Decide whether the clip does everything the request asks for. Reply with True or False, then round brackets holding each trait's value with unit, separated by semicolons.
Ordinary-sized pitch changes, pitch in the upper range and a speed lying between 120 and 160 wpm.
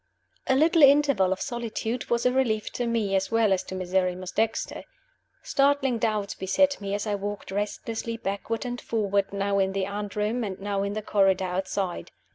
False (3.4 semitones; 205 Hz; 180 wpm)